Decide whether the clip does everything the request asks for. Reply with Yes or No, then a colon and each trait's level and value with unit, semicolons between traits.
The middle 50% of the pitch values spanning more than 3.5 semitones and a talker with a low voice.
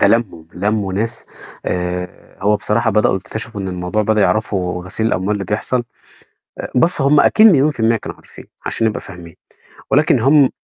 Yes: average, 3.9 semitones; low, 105 Hz